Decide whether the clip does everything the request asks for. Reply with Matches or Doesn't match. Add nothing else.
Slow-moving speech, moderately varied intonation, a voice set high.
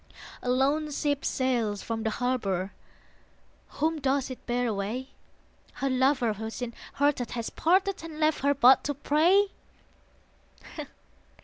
Matches